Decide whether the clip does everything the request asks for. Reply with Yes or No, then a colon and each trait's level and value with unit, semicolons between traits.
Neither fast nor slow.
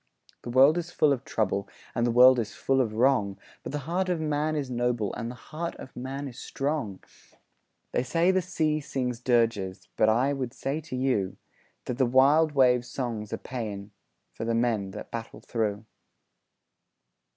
Yes: average, 180 wpm